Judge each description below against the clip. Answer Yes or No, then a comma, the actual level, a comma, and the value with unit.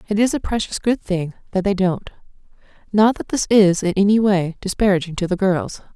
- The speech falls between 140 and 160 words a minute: No, average, 190 wpm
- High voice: Yes, high, 195 Hz